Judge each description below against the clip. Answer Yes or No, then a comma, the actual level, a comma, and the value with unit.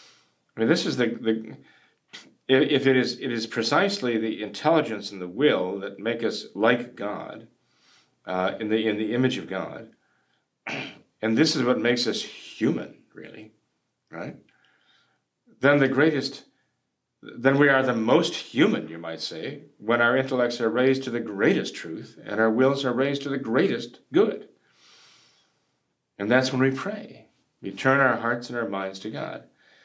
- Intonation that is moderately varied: Yes, average, 3.3 semitones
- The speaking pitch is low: Yes, low, 120 Hz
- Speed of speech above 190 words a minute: No, average, 165 wpm